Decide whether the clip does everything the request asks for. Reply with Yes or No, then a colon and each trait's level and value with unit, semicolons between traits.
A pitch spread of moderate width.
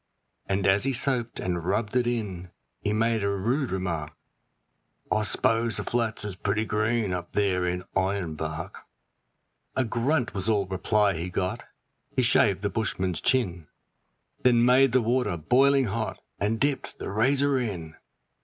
Yes: average, 4.4 semitones